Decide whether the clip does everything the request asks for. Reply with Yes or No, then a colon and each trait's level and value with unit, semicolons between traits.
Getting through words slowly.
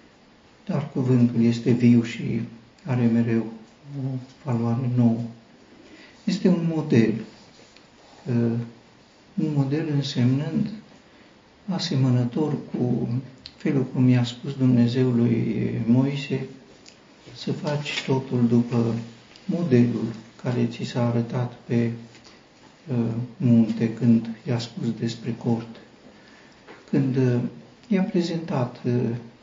Yes: slow, 90 wpm